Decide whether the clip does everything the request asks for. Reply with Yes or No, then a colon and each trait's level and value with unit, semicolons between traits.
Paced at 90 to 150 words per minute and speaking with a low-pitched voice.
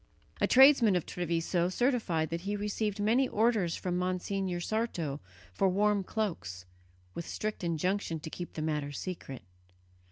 No: average, 140 wpm; medium, 185 Hz